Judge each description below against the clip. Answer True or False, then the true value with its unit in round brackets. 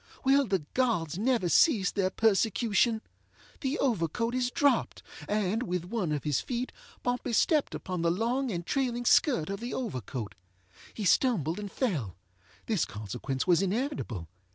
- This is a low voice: False (210 Hz)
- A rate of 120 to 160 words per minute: True (145 wpm)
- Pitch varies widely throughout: True (6.7 semitones)